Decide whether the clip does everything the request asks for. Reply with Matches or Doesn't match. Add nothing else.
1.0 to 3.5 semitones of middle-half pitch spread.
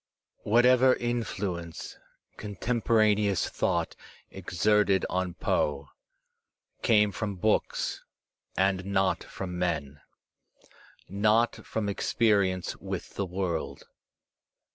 Matches